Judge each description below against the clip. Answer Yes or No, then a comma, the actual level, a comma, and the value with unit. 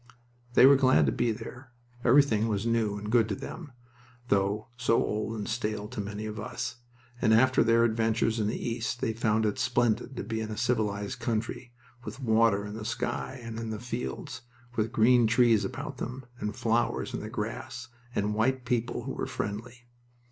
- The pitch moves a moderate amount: No, narrow, 2.2 semitones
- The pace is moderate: Yes, average, 190 wpm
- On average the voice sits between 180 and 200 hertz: No, low, 115 Hz